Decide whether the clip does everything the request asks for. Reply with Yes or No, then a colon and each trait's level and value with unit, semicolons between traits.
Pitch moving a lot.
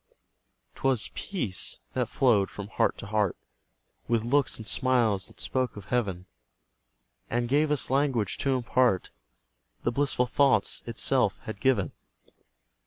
No: average, 4.3 semitones